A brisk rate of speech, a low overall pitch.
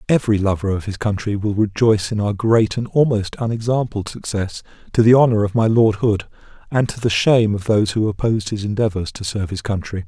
Yes: fast, 210 wpm; low, 105 Hz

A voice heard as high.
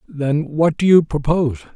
No: medium, 150 Hz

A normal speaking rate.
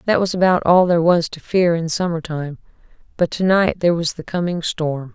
No: fast, 220 wpm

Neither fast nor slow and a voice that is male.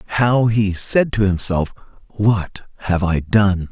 Yes: average, 145 wpm; male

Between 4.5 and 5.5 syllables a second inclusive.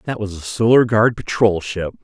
Yes: 5.1 syllables/s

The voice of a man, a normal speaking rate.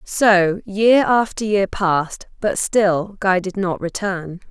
No: female; average, 145 wpm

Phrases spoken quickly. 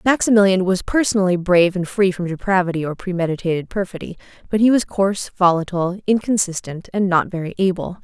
No: average, 155 wpm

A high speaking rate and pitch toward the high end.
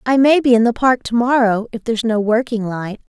Yes: fast, 265 wpm; high, 230 Hz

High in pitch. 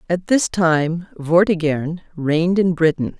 No: medium, 170 Hz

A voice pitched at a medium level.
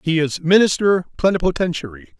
Yes: medium, 160 Hz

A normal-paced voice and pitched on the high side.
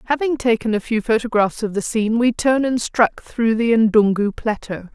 Yes: average, 195 wpm; high, 225 Hz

